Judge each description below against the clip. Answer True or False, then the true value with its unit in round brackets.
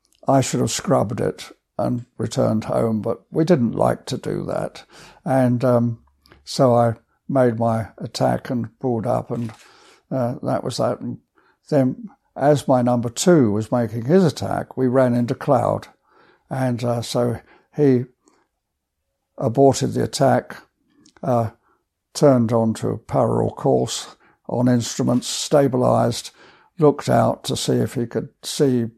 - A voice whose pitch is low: True (125 Hz)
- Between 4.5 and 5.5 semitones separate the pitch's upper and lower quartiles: False (2.7 semitones)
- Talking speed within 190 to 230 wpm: False (140 wpm)